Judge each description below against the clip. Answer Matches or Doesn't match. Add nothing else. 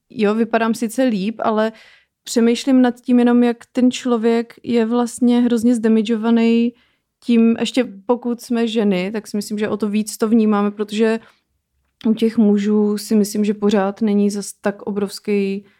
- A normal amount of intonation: Doesn't match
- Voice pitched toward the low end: Doesn't match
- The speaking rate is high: Doesn't match